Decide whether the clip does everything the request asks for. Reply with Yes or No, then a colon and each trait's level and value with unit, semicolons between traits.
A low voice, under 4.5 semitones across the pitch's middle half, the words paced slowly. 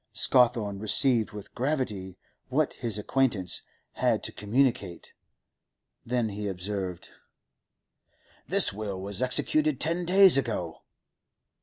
No: low, 110 Hz; average, 4.8 semitones; slow, 105 wpm